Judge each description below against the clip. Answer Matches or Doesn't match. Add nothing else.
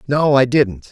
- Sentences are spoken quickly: Doesn't match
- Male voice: Matches